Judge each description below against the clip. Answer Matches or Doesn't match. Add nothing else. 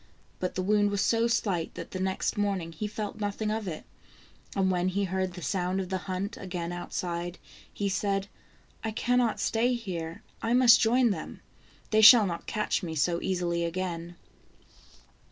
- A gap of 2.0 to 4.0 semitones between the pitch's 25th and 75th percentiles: Matches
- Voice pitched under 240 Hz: Matches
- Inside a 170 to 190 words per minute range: Matches